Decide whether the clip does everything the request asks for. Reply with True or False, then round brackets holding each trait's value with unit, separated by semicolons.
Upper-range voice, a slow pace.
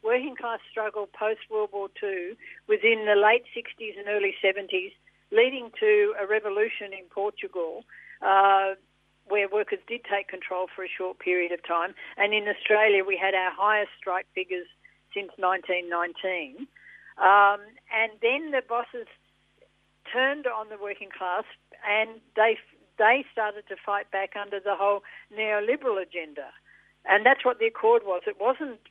False (210 Hz; 150 wpm)